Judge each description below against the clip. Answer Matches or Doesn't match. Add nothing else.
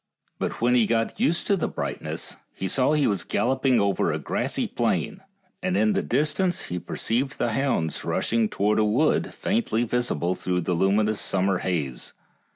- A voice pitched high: Doesn't match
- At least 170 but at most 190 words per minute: Matches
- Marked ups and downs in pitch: Matches